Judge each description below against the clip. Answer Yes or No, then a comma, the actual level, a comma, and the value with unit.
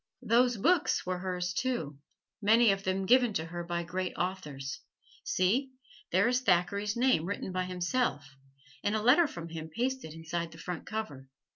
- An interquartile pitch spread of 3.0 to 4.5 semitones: No, wide, 5.6 semitones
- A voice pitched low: No, medium, 185 Hz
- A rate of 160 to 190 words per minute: Yes, average, 165 wpm